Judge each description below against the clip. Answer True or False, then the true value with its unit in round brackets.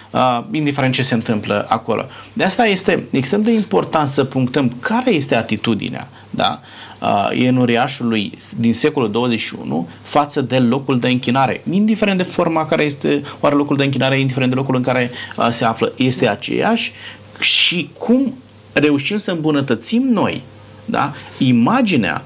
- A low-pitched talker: True (130 Hz)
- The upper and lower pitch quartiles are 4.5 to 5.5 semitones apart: True (5.0 semitones)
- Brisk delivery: False (150 wpm)